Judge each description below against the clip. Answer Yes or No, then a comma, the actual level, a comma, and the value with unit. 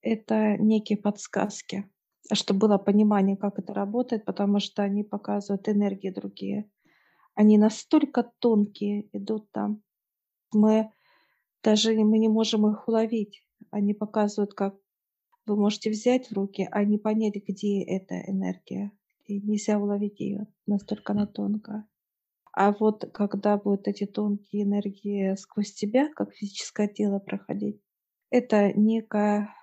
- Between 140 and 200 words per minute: No, average, 130 wpm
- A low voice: No, high, 210 Hz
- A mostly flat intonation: Yes, narrow, 1.1 semitones